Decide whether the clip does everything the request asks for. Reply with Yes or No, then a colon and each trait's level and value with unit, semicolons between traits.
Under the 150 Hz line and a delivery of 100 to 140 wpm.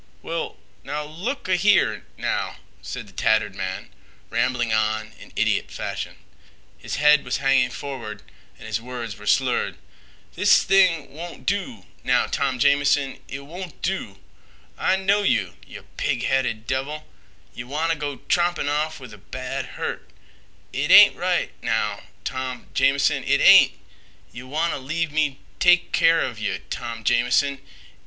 Yes: low, 135 Hz; slow, 135 wpm